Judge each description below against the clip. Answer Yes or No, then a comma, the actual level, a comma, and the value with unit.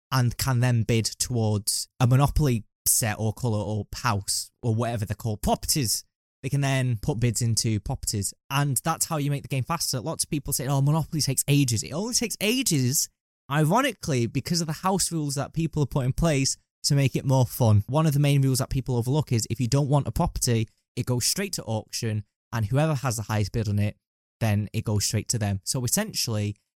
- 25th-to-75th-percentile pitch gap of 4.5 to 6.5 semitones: Yes, average, 5.0 semitones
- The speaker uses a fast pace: Yes, fast, 215 wpm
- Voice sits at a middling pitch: No, low, 130 Hz